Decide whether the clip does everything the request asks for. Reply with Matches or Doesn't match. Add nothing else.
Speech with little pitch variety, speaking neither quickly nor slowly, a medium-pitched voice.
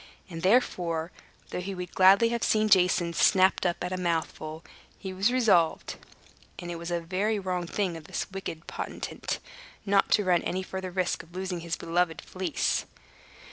Matches